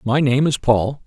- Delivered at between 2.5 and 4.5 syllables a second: Yes, 4.3 syllables/s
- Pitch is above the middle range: No, low, 130 Hz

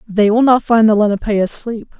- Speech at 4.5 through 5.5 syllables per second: Yes, 5.4 syllables/s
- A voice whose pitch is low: No, high, 220 Hz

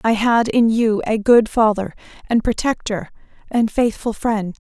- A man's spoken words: No, female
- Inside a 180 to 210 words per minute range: No, average, 155 wpm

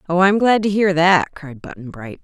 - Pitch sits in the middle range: Yes, medium, 175 Hz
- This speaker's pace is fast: Yes, fast, 240 wpm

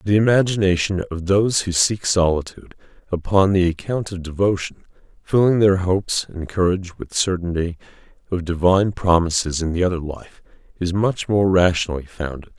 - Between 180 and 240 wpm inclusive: No, average, 150 wpm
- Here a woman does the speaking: No, male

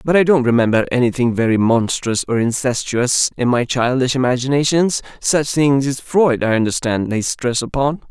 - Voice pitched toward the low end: Yes, low, 130 Hz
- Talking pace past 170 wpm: No, average, 155 wpm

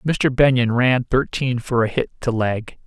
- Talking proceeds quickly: No, average, 190 wpm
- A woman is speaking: No, male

